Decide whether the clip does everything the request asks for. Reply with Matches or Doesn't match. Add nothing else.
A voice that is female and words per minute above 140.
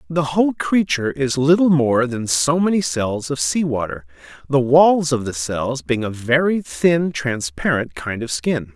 Doesn't match